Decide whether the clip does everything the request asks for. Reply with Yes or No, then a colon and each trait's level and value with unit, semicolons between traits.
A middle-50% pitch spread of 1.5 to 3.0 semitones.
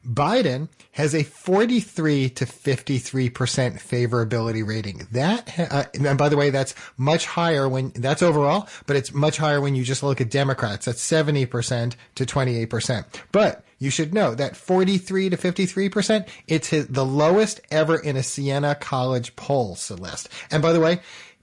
No: average, 4.1 semitones